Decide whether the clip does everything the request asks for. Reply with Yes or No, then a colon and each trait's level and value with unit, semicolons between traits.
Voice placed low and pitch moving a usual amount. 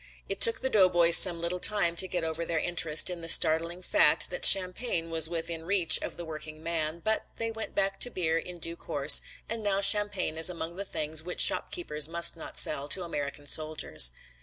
No: medium, 170 Hz; average, 3.0 semitones